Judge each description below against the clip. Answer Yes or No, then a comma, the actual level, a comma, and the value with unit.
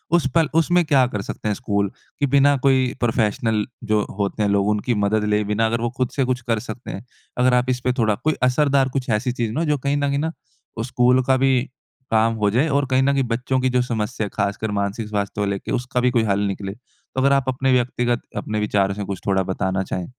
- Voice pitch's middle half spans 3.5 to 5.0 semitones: Yes, average, 3.9 semitones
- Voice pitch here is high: No, low, 120 Hz